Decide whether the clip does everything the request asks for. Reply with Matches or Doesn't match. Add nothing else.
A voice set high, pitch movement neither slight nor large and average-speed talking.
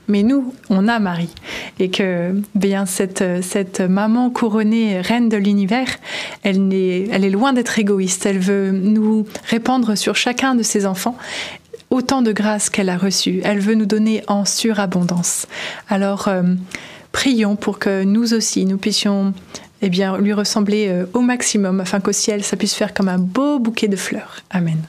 Doesn't match